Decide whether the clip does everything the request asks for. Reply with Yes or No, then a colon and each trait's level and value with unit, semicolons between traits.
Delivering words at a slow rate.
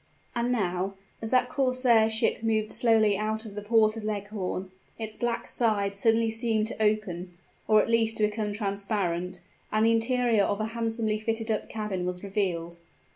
No: average, 175 wpm